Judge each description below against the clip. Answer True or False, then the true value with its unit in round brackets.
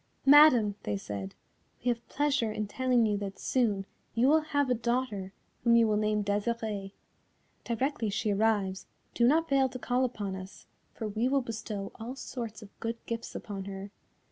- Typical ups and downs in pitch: True (3.8 semitones)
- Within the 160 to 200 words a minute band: True (175 wpm)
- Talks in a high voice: True (225 Hz)